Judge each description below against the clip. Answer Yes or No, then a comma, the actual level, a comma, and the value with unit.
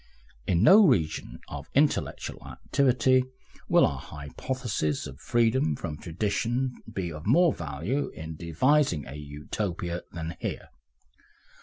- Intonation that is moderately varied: No, wide, 8.8 semitones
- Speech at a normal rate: No, slow, 120 wpm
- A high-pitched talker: No, very low, 90 Hz